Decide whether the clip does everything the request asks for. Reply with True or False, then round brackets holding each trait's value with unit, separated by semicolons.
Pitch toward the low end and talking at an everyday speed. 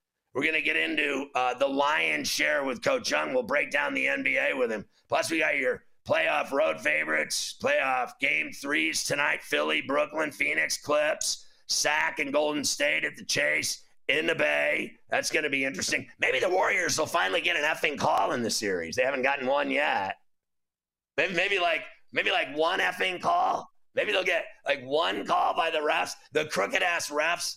False (155 Hz; 185 wpm)